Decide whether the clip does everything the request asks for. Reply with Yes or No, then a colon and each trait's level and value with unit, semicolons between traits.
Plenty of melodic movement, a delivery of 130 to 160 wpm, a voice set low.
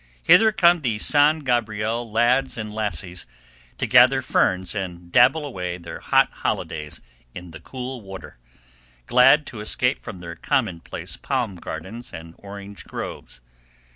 Yes: wide, 5.9 semitones; average, 140 wpm; low, 105 Hz